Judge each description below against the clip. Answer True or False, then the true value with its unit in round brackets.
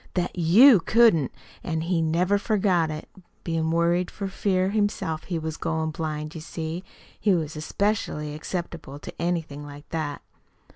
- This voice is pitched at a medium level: True (165 Hz)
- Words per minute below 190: True (150 wpm)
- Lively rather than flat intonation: False (2.8 semitones)